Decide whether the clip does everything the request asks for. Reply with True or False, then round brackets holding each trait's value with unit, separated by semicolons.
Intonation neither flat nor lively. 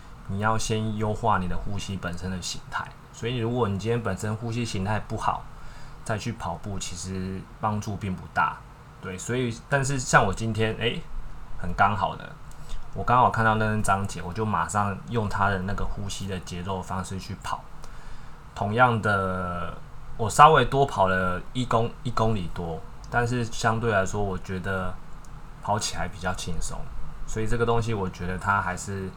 True (3.8 semitones)